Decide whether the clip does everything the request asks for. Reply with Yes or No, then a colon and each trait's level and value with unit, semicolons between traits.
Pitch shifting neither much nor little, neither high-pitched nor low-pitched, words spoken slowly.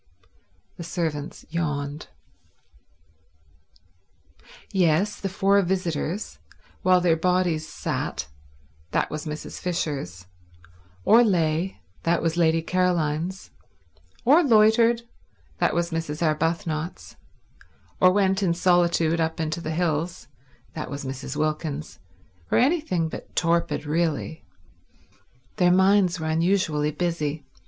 Yes: average, 3.7 semitones; medium, 165 Hz; slow, 90 wpm